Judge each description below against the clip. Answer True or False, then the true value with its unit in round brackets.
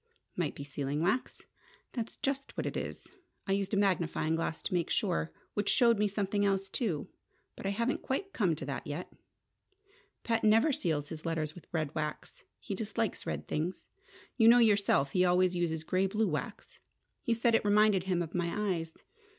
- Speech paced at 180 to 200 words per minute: True (185 wpm)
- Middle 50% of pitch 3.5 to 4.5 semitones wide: False (4.9 semitones)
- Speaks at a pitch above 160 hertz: True (185 Hz)